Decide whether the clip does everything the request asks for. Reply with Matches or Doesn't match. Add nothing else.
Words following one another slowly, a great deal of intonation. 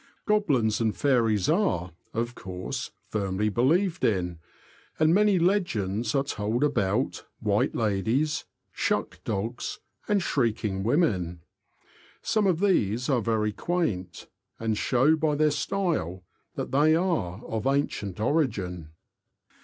Matches